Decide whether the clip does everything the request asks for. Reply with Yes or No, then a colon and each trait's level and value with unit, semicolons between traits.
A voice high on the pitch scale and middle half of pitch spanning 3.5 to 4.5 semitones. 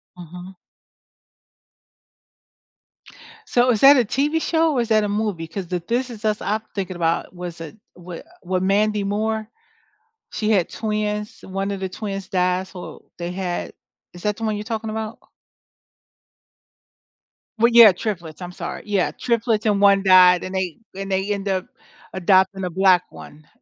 No: high, 195 Hz; average, 3.0 semitones